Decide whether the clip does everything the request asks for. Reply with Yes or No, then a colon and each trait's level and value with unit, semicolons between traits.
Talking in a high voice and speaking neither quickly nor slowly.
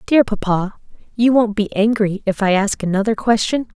Yes: high, 210 Hz; average, 175 wpm